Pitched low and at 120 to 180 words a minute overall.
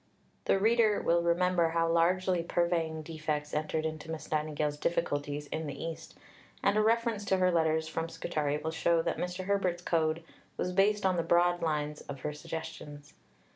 No: medium, 165 Hz; average, 175 wpm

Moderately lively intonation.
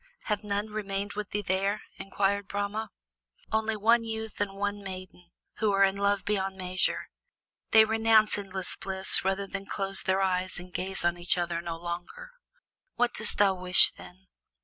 No: narrow, 2.0 semitones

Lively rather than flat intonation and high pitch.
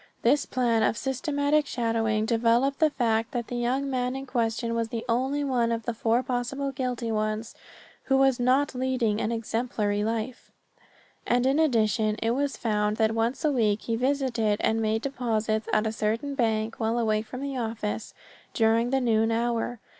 No: narrow, 2.6 semitones; high, 235 Hz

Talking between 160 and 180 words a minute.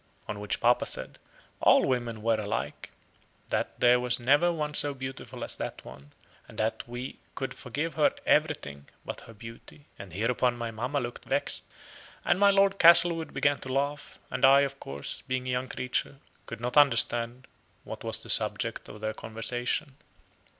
Yes: average, 170 wpm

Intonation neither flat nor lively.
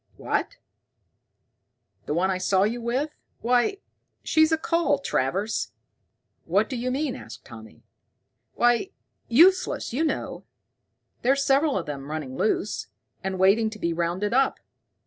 No: wide, 7.0 semitones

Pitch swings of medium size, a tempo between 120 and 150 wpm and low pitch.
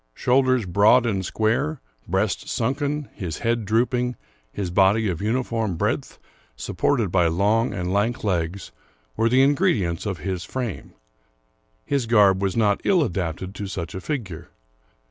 Yes: average, 4.7 semitones; average, 145 wpm; low, 105 Hz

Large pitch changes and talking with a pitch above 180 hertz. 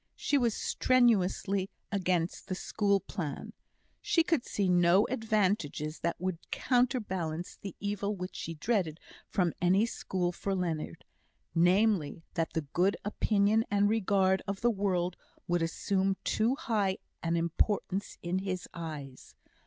No: average, 3.2 semitones; high, 190 Hz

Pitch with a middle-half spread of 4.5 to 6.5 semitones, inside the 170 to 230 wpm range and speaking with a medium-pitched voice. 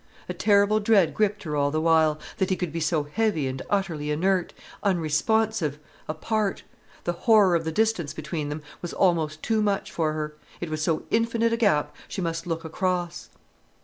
Yes: average, 4.8 semitones; average, 180 wpm; medium, 170 Hz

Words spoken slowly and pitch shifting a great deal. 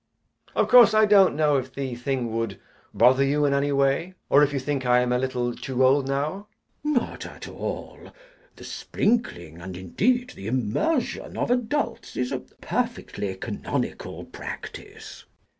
No: average, 160 wpm; wide, 8.4 semitones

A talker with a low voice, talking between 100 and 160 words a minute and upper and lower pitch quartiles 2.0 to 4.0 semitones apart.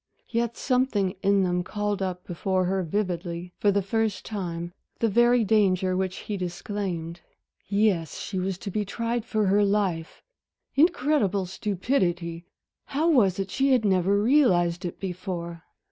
No: high, 195 Hz; average, 145 wpm; average, 3.3 semitones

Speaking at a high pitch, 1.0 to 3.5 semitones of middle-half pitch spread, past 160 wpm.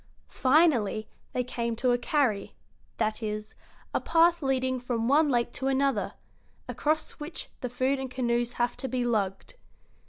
No: very high, 250 Hz; average, 2.7 semitones; average, 155 wpm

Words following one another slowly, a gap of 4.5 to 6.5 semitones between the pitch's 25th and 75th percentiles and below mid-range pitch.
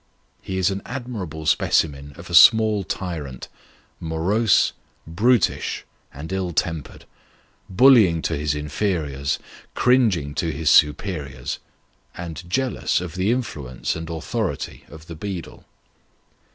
Yes: slow, 115 wpm; average, 5.0 semitones; very low, 85 Hz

